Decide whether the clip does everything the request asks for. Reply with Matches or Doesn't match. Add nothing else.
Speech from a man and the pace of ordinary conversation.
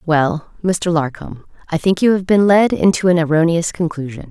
Doesn't match